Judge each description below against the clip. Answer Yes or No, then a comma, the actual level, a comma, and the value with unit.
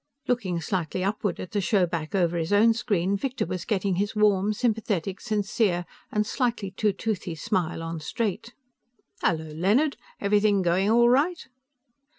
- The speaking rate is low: No, average, 150 wpm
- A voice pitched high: Yes, high, 200 Hz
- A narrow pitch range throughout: No, average, 3.7 semitones